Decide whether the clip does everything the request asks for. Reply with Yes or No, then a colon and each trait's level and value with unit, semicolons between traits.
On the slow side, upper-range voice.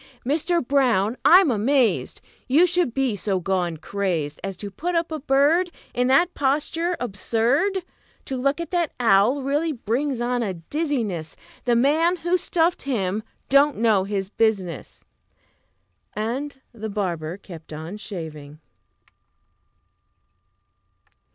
Yes: slow, 130 wpm; high, 245 Hz